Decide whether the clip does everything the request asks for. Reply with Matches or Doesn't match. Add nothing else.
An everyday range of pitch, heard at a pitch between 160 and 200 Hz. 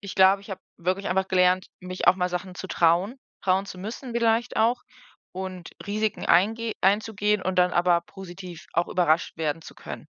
Doesn't match